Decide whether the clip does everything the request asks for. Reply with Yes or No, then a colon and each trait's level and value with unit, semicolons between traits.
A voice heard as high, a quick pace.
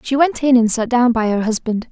Yes: high, 240 Hz; fast, 280 wpm